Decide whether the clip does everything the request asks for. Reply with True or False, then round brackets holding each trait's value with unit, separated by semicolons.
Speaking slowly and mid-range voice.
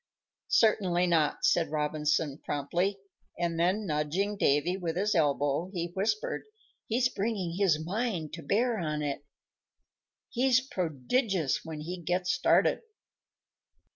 True (115 wpm; 175 Hz)